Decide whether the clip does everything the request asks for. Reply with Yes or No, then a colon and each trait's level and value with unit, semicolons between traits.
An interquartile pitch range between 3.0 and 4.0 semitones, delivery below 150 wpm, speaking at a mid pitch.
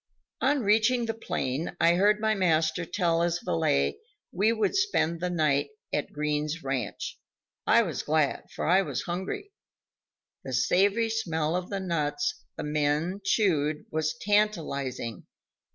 No: wide, 5.6 semitones; average, 140 wpm; medium, 170 Hz